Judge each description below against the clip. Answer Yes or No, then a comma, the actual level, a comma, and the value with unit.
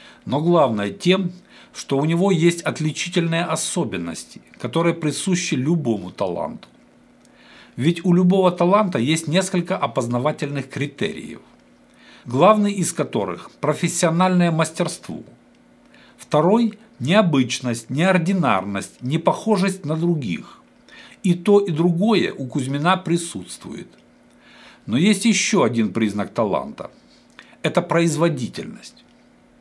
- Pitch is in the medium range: Yes, medium, 170 Hz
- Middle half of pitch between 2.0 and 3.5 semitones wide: No, average, 4.5 semitones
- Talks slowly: Yes, slow, 95 wpm